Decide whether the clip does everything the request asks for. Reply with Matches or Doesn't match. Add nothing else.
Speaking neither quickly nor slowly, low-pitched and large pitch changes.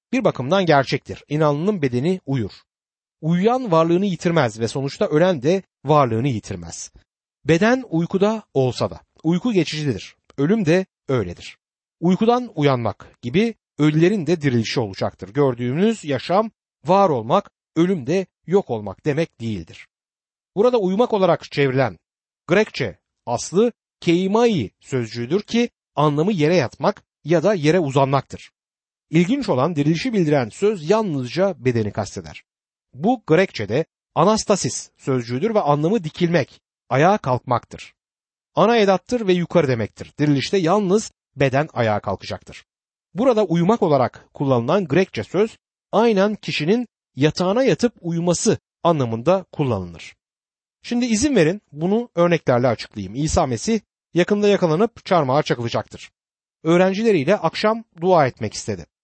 Doesn't match